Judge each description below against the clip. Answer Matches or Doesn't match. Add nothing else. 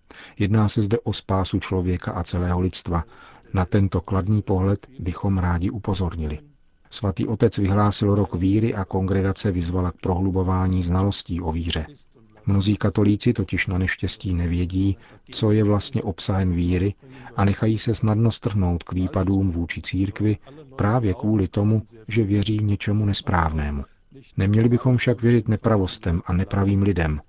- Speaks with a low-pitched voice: Matches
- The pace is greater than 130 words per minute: Matches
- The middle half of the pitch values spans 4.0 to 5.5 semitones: Doesn't match